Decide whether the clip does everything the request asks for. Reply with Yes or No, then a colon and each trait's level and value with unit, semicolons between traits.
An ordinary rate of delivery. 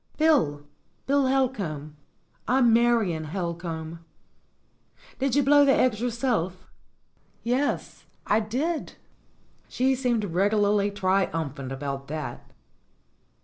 No: slow, 95 wpm